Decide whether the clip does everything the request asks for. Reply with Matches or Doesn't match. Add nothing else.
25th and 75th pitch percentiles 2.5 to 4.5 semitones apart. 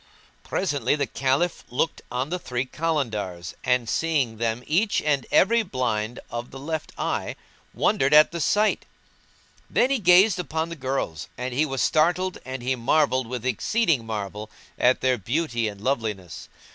Doesn't match